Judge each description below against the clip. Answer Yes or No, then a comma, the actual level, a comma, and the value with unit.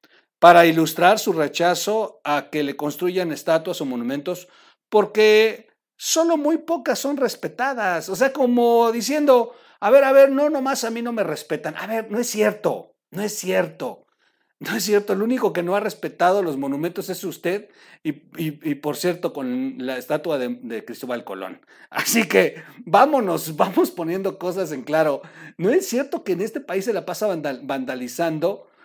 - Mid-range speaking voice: No, high, 200 Hz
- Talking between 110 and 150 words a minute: No, average, 175 wpm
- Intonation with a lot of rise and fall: Yes, wide, 7.2 semitones